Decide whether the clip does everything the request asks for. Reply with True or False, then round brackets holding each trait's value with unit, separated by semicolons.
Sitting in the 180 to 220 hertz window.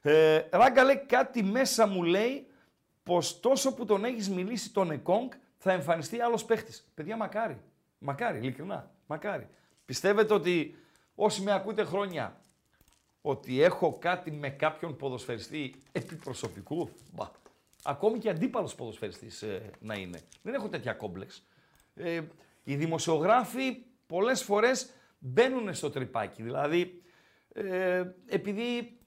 True (185 Hz)